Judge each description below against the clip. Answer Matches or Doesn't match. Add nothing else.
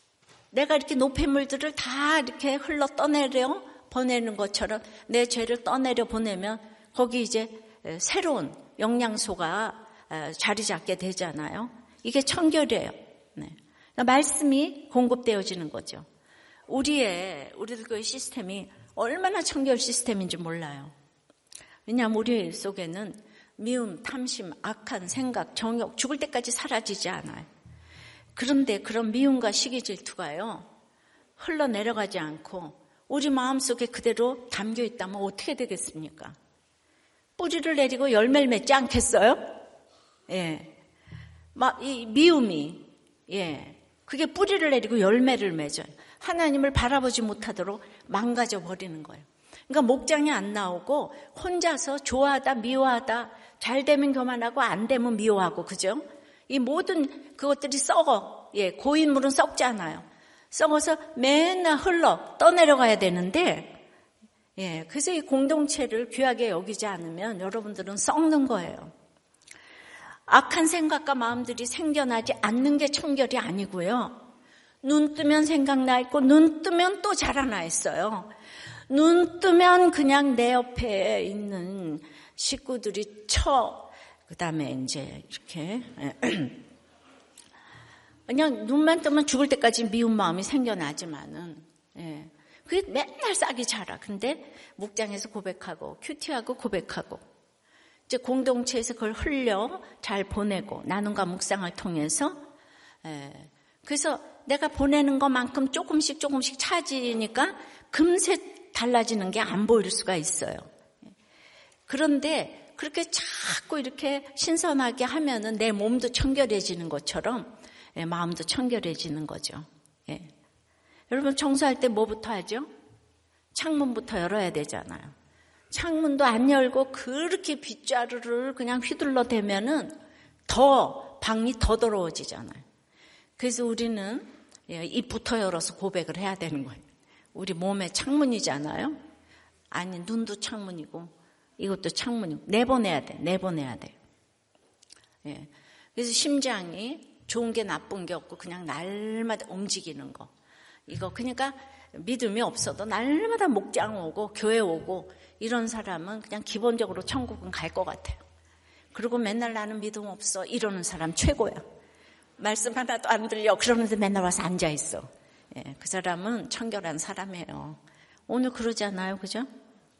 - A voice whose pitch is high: Matches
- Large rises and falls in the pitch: Matches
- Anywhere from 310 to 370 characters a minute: Doesn't match